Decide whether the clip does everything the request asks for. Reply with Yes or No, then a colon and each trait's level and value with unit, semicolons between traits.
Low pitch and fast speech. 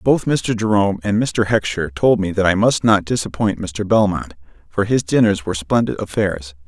No: low, 100 Hz; average, 190 wpm